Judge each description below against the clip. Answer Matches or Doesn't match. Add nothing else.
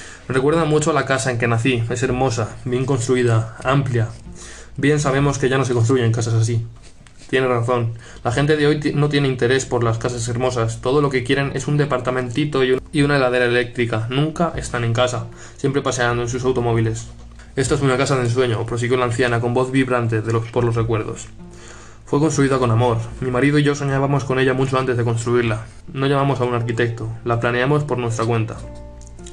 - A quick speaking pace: Matches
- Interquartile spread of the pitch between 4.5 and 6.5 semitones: Doesn't match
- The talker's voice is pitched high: Doesn't match